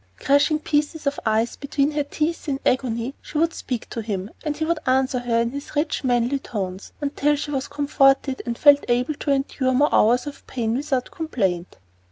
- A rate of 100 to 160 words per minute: No, average, 195 wpm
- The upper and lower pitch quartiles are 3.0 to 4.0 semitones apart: Yes, average, 3.5 semitones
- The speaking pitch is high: Yes, very high, 275 Hz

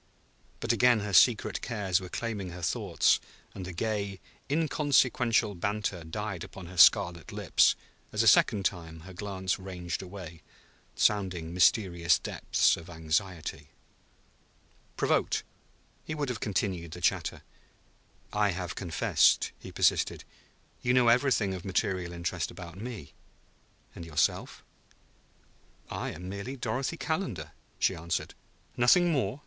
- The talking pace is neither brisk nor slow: No, slow, 130 wpm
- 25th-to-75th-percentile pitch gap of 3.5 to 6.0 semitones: Yes, average, 4.5 semitones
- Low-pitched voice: Yes, very low, 95 Hz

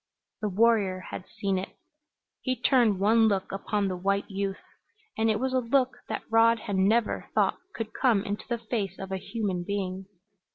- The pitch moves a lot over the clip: No, average, 3.0 semitones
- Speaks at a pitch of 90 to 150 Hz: No, high, 205 Hz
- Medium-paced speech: Yes, average, 180 wpm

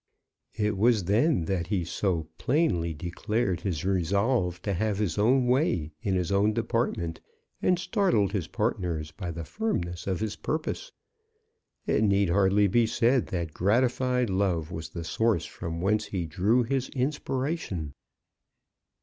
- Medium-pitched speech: No, low, 100 Hz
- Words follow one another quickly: No, average, 145 wpm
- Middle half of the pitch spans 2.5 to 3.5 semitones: No, wide, 5.5 semitones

